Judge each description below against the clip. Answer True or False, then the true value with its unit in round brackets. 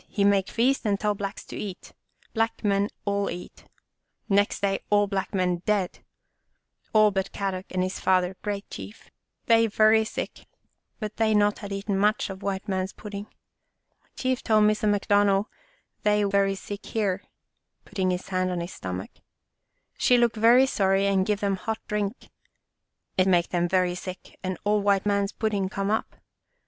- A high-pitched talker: True (200 Hz)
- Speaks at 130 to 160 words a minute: False (175 wpm)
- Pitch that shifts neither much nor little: False (1.7 semitones)